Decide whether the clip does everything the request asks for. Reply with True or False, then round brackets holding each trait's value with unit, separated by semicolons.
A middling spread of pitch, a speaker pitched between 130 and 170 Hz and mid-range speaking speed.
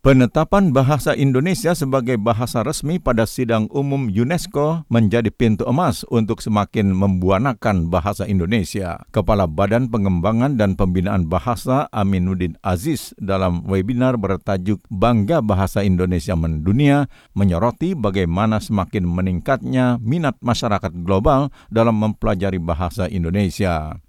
False (4.9 semitones; 105 Hz; 110 wpm)